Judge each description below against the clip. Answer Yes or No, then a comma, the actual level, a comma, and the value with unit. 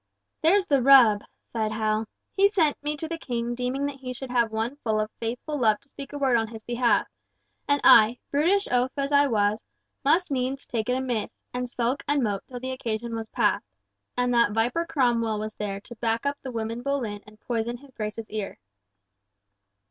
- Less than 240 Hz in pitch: No, high, 245 Hz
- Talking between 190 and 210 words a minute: Yes, average, 200 wpm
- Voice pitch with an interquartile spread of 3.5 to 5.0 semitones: Yes, average, 3.8 semitones